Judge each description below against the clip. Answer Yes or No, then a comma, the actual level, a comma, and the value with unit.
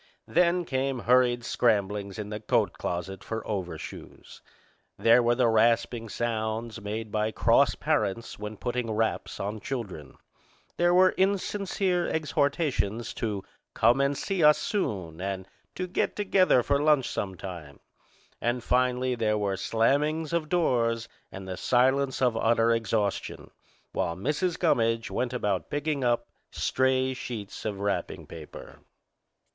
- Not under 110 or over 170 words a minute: Yes, average, 140 wpm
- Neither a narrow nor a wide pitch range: Yes, average, 4.7 semitones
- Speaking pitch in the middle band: No, low, 120 Hz